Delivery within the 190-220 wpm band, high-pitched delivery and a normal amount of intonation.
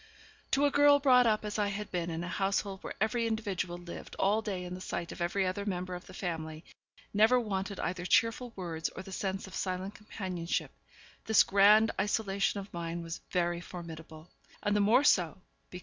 Yes: average, 200 wpm; high, 195 Hz; average, 3.2 semitones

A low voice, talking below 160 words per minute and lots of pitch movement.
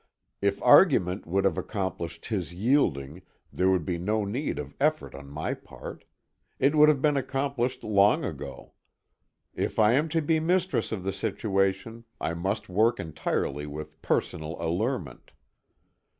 Yes: low, 100 Hz; average, 150 wpm; wide, 7.3 semitones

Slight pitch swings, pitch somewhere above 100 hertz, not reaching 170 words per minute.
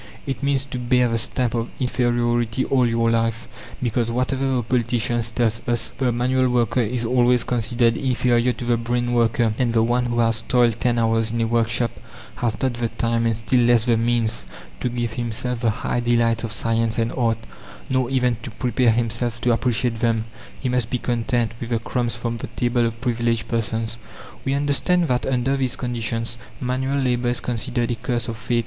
No: narrow, 1.3 semitones; low, 120 Hz; average, 195 wpm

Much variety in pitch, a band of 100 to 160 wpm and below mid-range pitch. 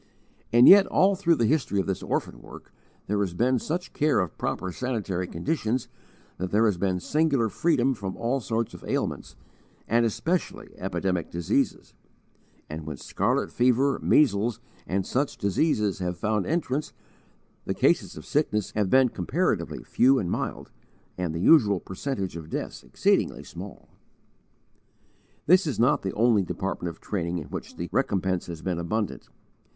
Yes: wide, 6.4 semitones; average, 155 wpm; low, 110 Hz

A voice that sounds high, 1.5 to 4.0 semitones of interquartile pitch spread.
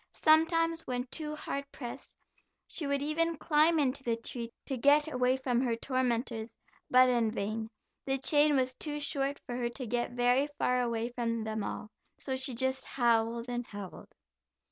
Yes: very high, 255 Hz; average, 3.3 semitones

